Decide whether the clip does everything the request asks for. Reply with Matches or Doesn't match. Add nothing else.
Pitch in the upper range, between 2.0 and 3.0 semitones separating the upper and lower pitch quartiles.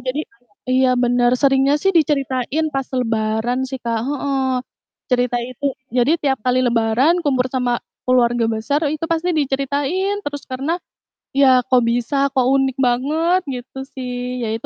Matches